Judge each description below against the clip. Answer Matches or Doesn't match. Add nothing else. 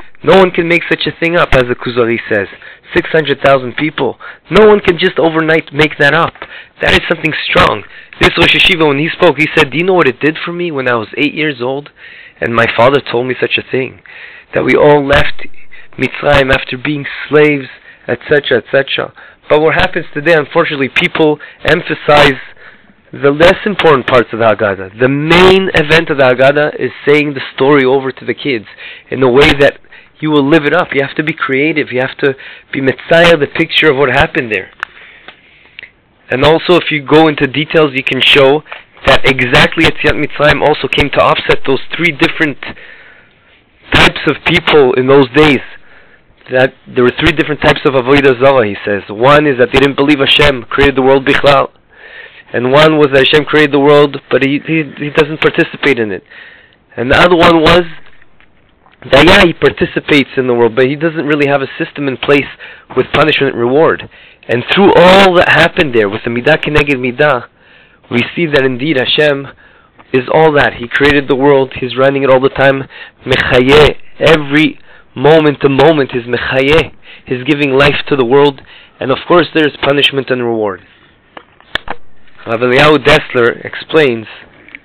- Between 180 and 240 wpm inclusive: Matches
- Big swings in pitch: Doesn't match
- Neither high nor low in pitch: Matches